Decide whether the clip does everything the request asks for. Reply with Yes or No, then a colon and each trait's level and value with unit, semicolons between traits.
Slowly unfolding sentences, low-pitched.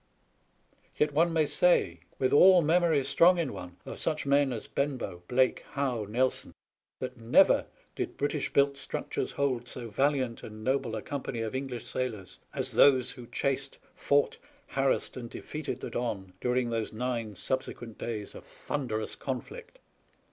No: average, 155 wpm; low, 130 Hz